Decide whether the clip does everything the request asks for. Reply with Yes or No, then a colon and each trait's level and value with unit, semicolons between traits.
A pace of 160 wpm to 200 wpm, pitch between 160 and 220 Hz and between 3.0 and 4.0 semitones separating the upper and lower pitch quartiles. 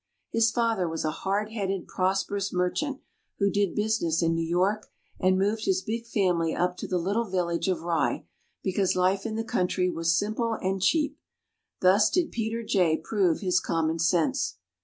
Yes: average, 170 wpm; high, 190 Hz; average, 3.6 semitones